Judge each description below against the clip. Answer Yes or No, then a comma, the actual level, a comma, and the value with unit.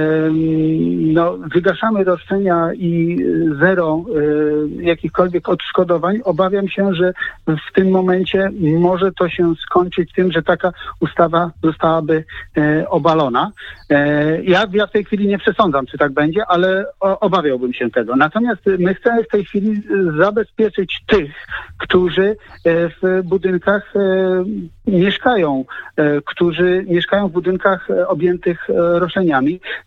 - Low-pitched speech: No, medium, 180 Hz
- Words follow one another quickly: No, slow, 110 wpm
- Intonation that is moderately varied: Yes, average, 3.0 semitones